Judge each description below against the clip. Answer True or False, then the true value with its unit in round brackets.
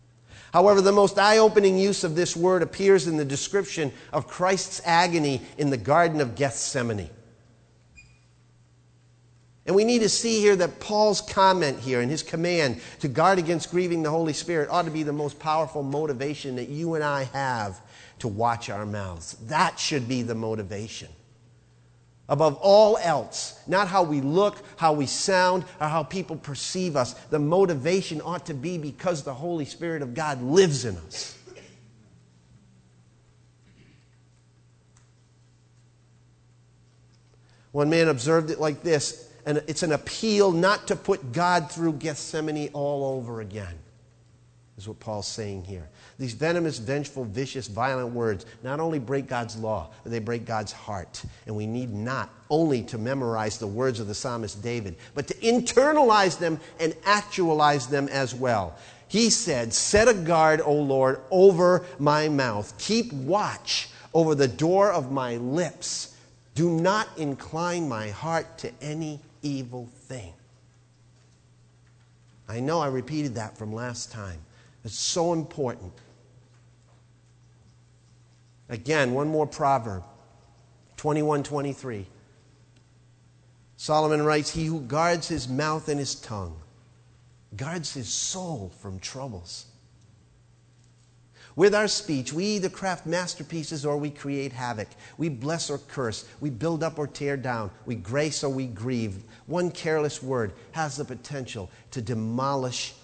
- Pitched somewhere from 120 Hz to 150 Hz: True (135 Hz)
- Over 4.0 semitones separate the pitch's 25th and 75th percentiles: True (5.5 semitones)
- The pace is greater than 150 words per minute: False (145 wpm)